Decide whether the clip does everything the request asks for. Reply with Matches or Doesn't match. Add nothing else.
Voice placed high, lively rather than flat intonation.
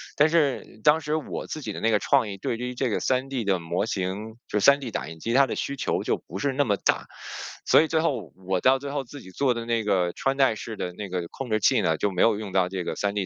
Doesn't match